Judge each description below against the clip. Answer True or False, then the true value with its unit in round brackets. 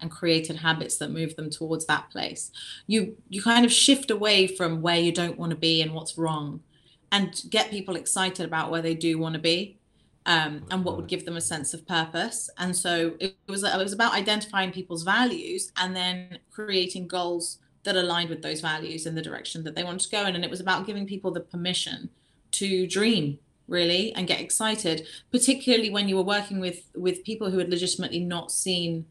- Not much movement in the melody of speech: False (3.1 semitones)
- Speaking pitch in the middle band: True (180 Hz)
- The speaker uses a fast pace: True (210 wpm)